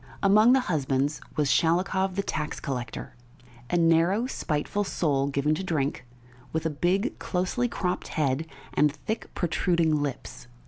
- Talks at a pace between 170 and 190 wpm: No, average, 140 wpm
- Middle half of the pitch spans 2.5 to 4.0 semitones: No, average, 4.6 semitones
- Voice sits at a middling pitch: Yes, medium, 165 Hz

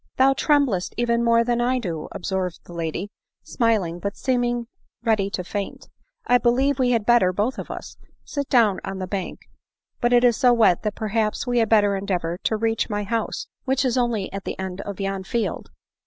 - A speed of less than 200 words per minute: No, fast, 205 wpm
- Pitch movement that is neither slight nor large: Yes, average, 3.8 semitones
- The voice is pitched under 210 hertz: No, high, 225 Hz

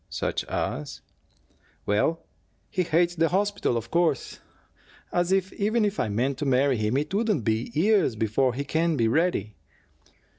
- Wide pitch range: Yes, wide, 7.6 semitones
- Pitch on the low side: No, medium, 155 Hz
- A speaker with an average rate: Yes, average, 160 wpm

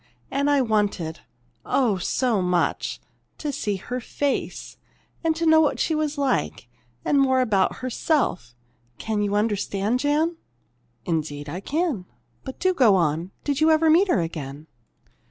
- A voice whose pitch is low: No, high, 245 Hz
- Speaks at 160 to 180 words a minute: No, average, 145 wpm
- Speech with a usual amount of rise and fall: No, wide, 8.0 semitones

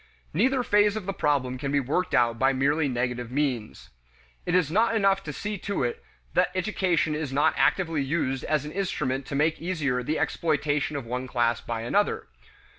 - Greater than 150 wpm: Yes, average, 190 wpm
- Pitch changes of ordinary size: No, wide, 5.9 semitones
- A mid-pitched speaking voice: Yes, medium, 150 Hz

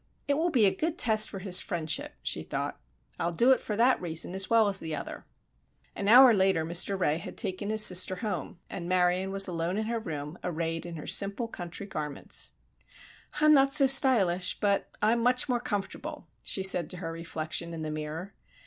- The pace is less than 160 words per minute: No, average, 200 wpm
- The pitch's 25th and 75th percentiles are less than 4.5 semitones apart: No, average, 4.9 semitones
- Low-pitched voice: No, high, 190 Hz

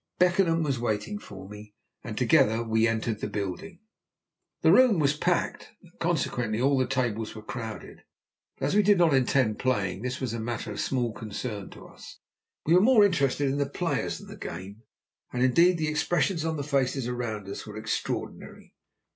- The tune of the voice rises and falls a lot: Yes, wide, 6.6 semitones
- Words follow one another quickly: No, average, 185 wpm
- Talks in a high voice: No, low, 130 Hz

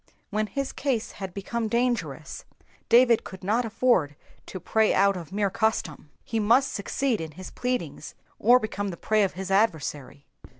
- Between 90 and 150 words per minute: No, average, 165 wpm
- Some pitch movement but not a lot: Yes, average, 4.0 semitones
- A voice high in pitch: Yes, high, 210 Hz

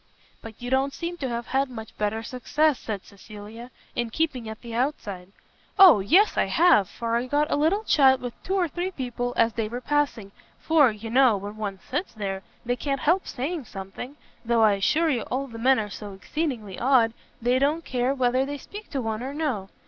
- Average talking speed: No, fast, 210 wpm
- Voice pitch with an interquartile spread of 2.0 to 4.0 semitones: No, average, 4.7 semitones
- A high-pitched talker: Yes, high, 245 Hz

